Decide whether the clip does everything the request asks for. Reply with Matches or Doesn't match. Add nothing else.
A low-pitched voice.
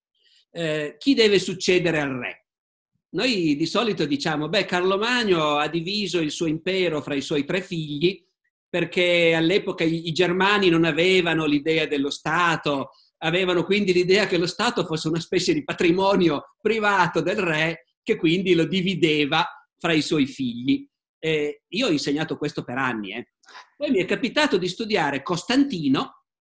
Doesn't match